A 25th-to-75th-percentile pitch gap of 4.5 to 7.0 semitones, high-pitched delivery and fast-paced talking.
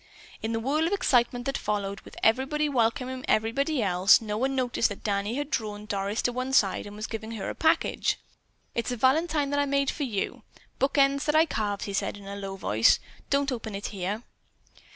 Yes: average, 5.1 semitones; high, 235 Hz; fast, 210 wpm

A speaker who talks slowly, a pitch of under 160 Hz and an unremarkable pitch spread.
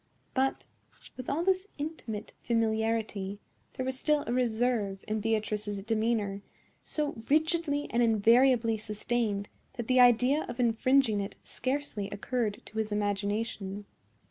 No: slow, 125 wpm; high, 230 Hz; average, 3.6 semitones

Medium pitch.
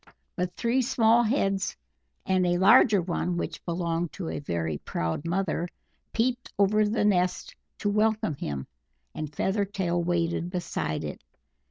Yes: medium, 180 Hz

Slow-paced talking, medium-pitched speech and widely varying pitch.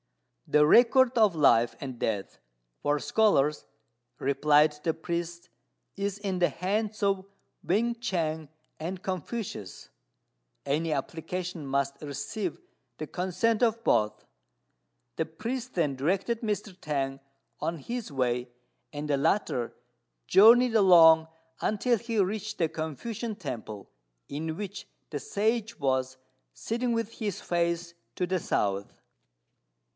Yes: slow, 120 wpm; medium, 175 Hz; wide, 6.4 semitones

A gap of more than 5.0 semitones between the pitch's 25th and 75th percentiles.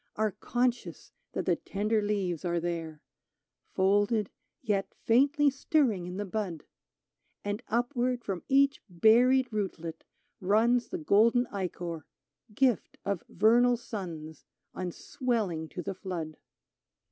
Yes: wide, 5.4 semitones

